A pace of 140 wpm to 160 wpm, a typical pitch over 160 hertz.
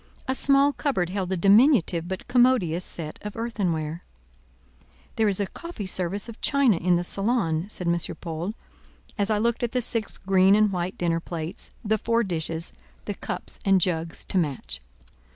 No: average, 170 wpm; high, 190 Hz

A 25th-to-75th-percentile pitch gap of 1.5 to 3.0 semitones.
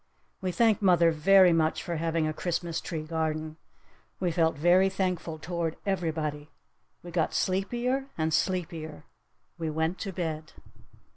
Yes: average, 2.7 semitones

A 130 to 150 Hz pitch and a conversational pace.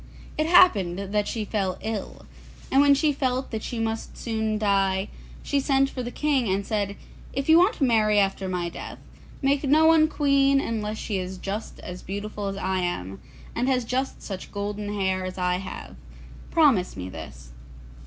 No: high, 215 Hz; average, 185 wpm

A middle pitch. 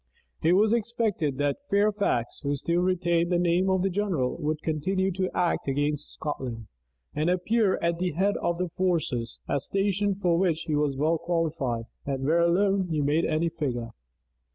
Yes: medium, 170 Hz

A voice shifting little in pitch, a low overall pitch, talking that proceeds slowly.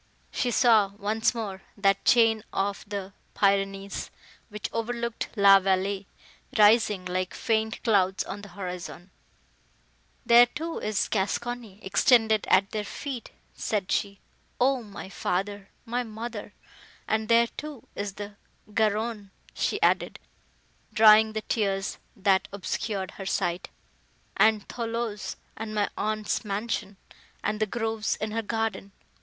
No: narrow, 2.3 semitones; high, 210 Hz; slow, 120 wpm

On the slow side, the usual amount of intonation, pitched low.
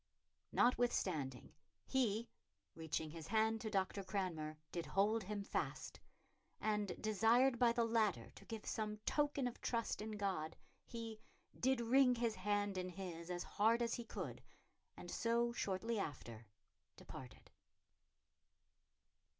No: slow, 130 wpm; average, 4.0 semitones; high, 215 Hz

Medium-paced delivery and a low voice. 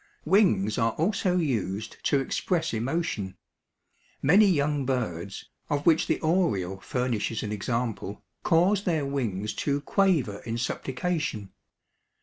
No: slow, 120 wpm; low, 130 Hz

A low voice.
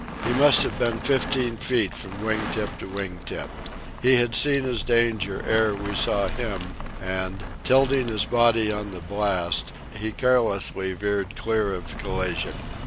Yes: low, 105 Hz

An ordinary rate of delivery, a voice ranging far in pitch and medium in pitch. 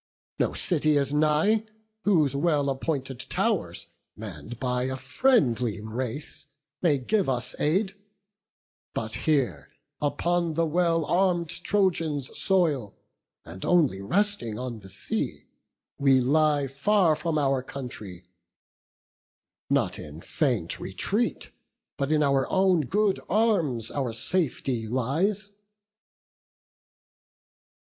No: slow, 105 wpm; wide, 5.8 semitones; medium, 145 Hz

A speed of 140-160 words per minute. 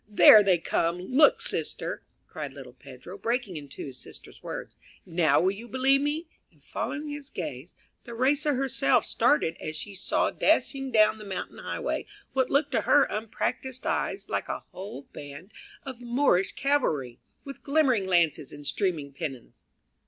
Yes: average, 155 wpm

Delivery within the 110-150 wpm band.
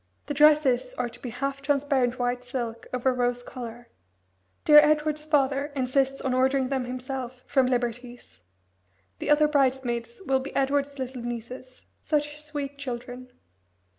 Yes: average, 140 wpm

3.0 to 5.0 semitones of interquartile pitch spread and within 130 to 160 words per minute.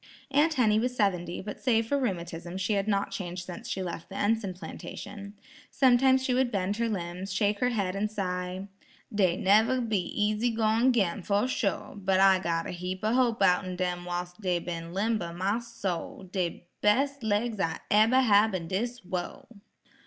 No: average, 3.9 semitones; average, 180 wpm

